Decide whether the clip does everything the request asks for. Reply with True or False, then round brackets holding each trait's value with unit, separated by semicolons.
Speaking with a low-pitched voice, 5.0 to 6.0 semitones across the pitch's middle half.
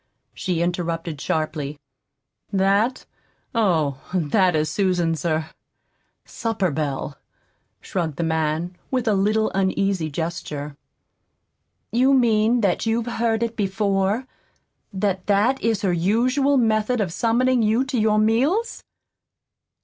False (195 Hz; 5.4 semitones)